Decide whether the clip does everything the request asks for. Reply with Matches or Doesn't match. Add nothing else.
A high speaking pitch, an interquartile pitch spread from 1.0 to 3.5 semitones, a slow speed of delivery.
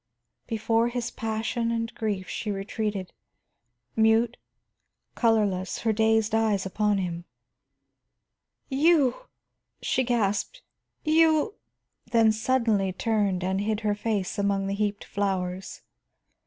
Matches